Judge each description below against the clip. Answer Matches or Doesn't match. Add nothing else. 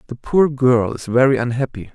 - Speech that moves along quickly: Doesn't match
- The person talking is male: Matches